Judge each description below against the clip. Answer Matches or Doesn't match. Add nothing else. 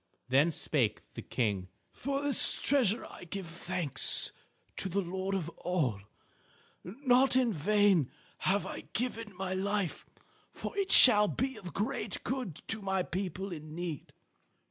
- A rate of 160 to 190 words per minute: Doesn't match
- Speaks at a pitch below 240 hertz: Matches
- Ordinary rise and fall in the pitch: Matches